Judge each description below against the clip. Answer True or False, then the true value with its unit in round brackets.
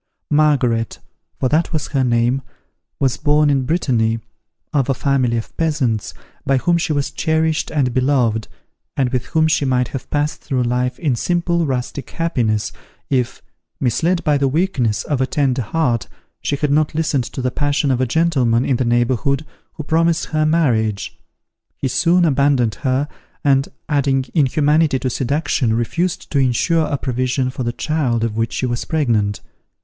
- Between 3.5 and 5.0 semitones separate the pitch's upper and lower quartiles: True (3.8 semitones)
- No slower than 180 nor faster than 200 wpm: False (165 wpm)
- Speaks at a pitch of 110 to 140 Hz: True (135 Hz)